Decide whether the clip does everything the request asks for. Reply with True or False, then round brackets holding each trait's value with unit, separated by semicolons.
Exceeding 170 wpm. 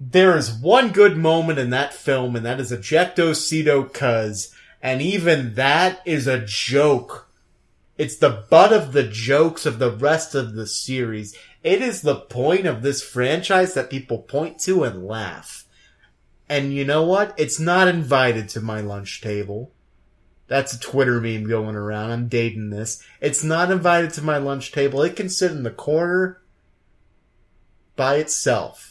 False (165 wpm)